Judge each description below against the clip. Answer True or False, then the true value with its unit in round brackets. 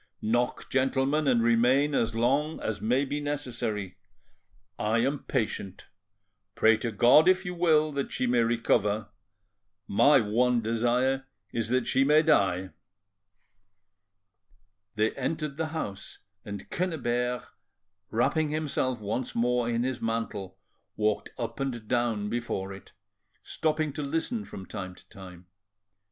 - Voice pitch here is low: True (120 Hz)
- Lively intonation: False (4.4 semitones)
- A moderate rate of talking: False (130 wpm)